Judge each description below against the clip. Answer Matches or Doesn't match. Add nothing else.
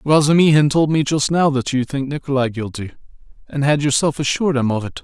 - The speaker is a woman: Doesn't match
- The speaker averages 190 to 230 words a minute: Matches